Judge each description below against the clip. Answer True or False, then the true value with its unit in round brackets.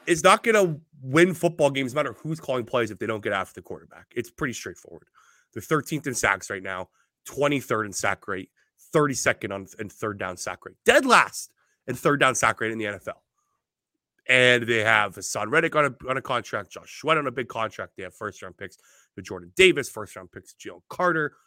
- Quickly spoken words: True (215 wpm)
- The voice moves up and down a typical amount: False (6.3 semitones)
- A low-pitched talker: True (130 Hz)